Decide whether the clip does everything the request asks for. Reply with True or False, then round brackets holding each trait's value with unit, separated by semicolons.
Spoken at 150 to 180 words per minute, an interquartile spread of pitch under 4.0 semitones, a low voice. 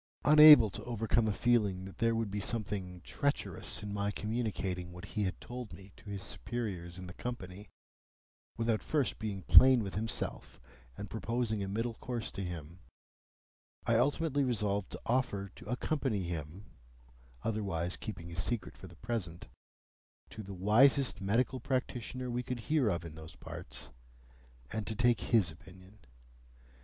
False (155 wpm; 4.4 semitones; 105 Hz)